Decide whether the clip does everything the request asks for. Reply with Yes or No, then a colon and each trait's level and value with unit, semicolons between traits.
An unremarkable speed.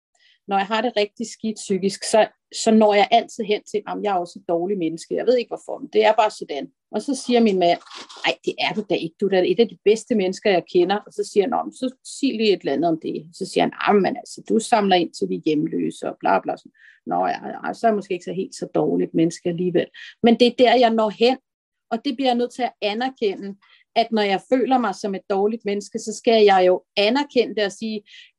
No: fast, 270 wpm